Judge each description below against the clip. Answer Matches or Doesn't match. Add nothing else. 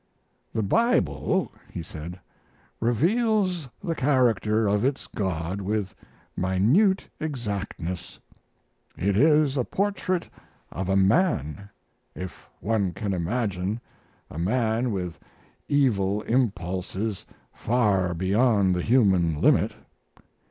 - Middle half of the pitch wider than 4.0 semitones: Matches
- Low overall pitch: Matches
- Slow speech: Matches